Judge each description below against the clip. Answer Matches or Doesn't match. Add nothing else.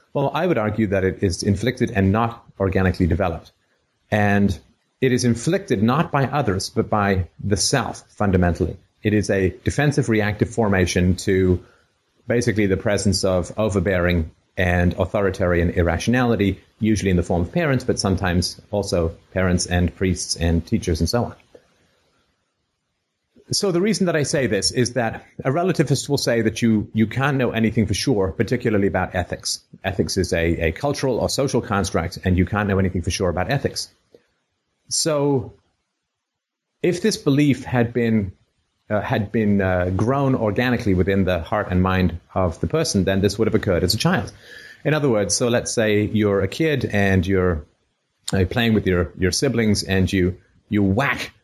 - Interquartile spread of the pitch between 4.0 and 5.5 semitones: Matches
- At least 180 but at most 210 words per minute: Doesn't match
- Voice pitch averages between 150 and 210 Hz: Doesn't match